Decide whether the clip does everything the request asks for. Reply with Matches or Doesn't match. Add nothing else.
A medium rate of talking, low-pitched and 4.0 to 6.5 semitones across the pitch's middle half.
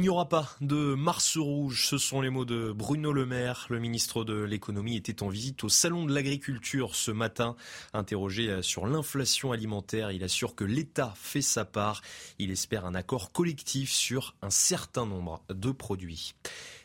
Matches